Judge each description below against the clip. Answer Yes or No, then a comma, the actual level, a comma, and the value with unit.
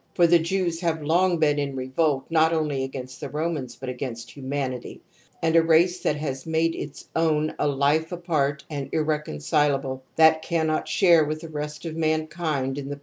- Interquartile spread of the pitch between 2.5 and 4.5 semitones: Yes, average, 2.9 semitones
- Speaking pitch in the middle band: Yes, medium, 155 Hz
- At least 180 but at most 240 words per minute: Yes, average, 185 wpm